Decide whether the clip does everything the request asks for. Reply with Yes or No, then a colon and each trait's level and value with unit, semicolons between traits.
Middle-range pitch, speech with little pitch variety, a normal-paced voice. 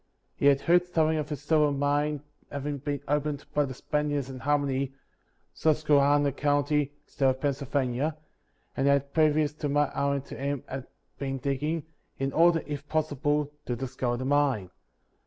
Yes: medium, 145 Hz; narrow, 1.5 semitones; average, 155 wpm